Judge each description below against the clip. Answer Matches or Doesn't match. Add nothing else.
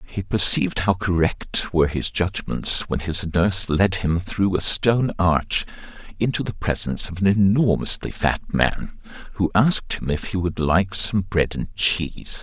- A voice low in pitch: Matches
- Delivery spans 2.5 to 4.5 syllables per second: Matches